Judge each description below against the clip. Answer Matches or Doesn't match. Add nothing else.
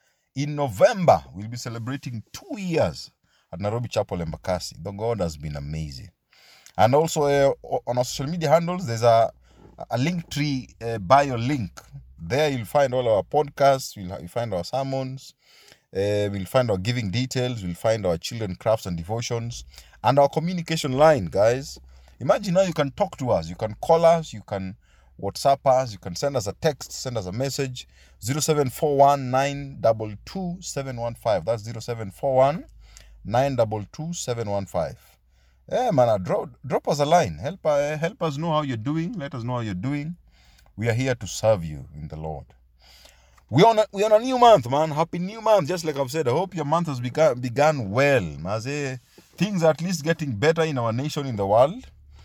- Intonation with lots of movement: Matches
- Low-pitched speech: Matches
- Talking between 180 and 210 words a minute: Matches